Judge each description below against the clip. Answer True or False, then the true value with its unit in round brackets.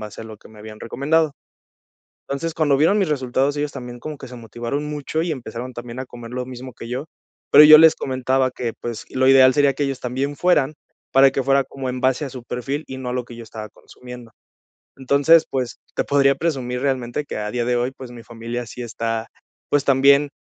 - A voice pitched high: False (130 Hz)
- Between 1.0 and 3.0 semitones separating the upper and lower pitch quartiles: True (2.6 semitones)